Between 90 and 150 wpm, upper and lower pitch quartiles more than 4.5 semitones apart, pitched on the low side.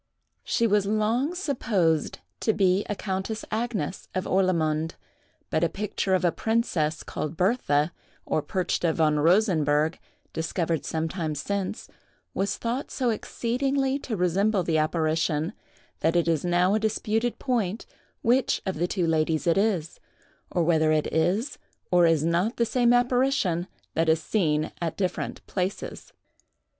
No: average, 145 wpm; average, 5.2 semitones; medium, 185 Hz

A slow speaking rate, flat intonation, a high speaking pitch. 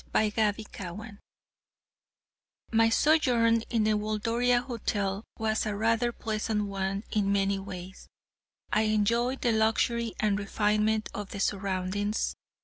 Yes: slow, 120 wpm; narrow, 2.1 semitones; high, 215 Hz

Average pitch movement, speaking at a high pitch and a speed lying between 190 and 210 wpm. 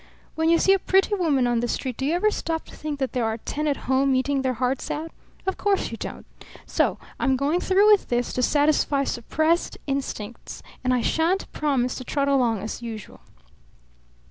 Yes: average, 4.3 semitones; very high, 275 Hz; average, 200 wpm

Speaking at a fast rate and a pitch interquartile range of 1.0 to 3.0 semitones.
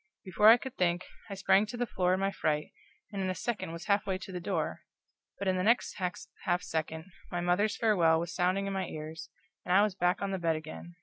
Yes: fast, 240 wpm; narrow, 2.5 semitones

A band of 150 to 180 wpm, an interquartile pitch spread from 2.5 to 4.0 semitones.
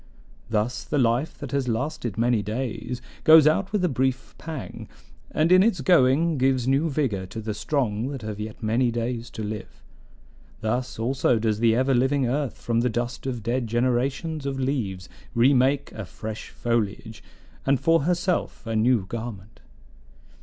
Yes: average, 165 wpm; average, 3.6 semitones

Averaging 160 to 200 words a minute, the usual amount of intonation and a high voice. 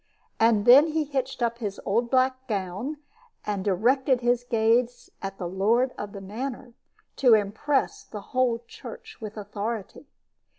No: average, 145 wpm; average, 3.9 semitones; high, 235 Hz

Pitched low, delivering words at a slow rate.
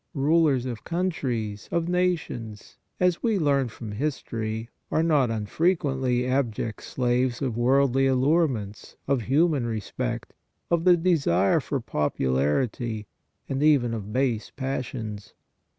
Yes: low, 130 Hz; slow, 120 wpm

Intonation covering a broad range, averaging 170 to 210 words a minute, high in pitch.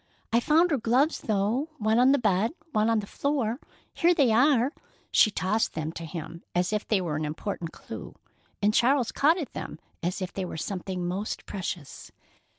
Yes: wide, 6.3 semitones; average, 190 wpm; high, 215 Hz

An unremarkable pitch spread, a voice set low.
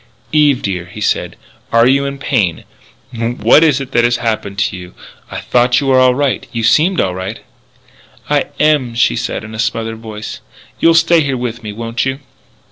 Yes: average, 3.9 semitones; low, 120 Hz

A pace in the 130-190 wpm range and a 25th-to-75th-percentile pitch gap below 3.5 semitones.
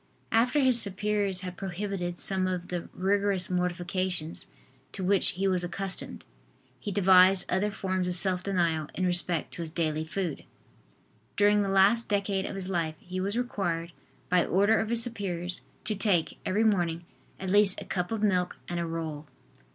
Yes: average, 170 wpm; narrow, 2.4 semitones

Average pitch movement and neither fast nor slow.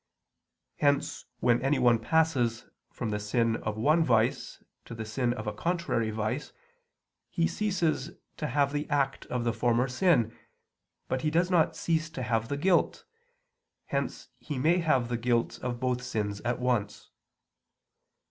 Yes: average, 4.8 semitones; average, 155 wpm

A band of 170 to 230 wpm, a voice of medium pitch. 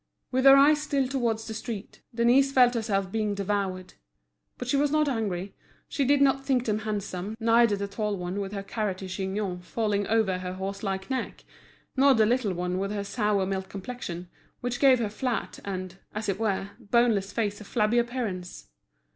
No: average, 185 wpm; high, 210 Hz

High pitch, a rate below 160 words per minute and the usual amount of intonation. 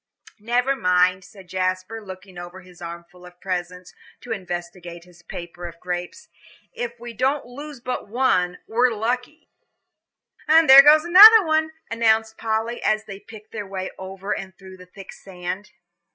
Yes: high, 195 Hz; average, 150 wpm; average, 5.0 semitones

